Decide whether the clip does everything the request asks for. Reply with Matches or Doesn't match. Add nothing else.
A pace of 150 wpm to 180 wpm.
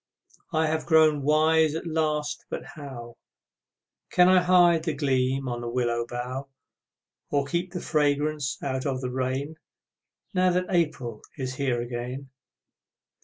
Doesn't match